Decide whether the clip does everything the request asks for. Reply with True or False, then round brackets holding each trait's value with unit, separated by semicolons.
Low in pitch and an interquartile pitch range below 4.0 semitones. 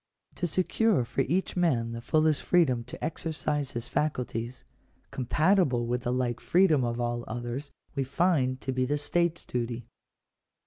False (130 Hz; 4.9 semitones)